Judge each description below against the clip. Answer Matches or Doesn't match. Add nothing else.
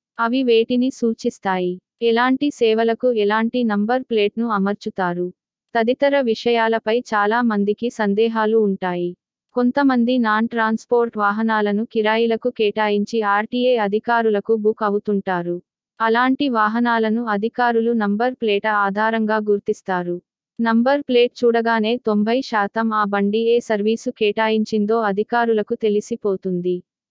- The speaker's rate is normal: Matches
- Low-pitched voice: Doesn't match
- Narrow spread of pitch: Matches